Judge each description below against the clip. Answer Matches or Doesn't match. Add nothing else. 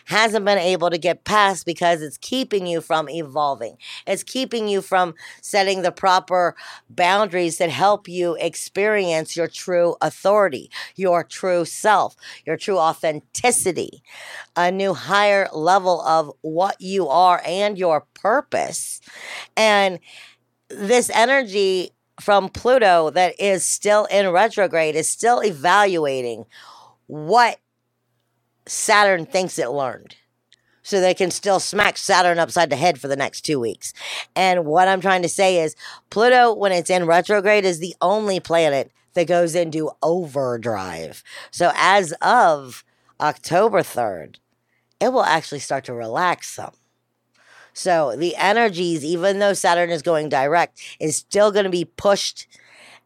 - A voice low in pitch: Doesn't match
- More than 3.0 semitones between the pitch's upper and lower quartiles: Matches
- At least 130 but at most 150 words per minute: Matches